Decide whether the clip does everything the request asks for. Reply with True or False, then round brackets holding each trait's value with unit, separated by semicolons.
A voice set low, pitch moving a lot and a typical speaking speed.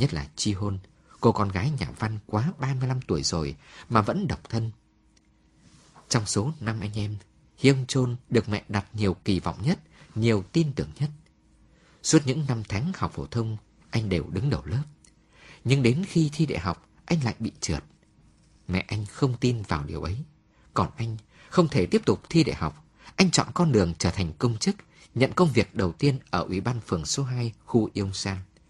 True (115 Hz; 5.9 semitones; 200 wpm)